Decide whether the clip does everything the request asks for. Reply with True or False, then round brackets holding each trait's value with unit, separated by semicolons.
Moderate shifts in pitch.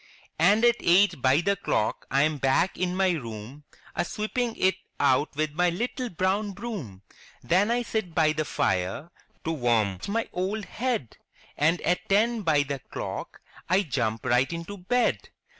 False (6.4 semitones)